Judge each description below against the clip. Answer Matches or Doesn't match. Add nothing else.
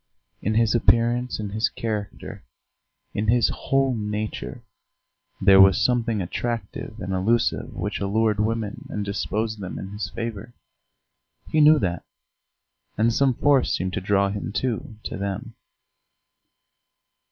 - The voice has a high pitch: Doesn't match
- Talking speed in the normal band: Doesn't match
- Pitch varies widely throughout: Doesn't match